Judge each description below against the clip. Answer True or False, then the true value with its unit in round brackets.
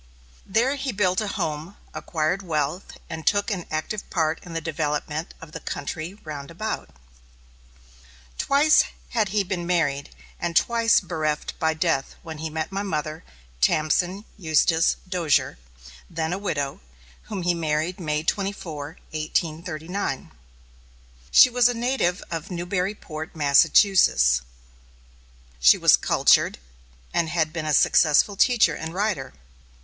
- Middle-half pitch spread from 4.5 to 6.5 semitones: False (4.0 semitones)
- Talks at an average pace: False (130 wpm)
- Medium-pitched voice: True (165 Hz)